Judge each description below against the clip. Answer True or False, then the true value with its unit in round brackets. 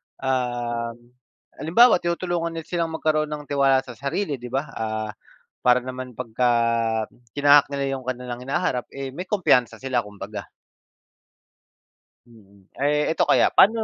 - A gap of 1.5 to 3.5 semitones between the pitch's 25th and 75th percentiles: False (4.0 semitones)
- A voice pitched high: False (130 Hz)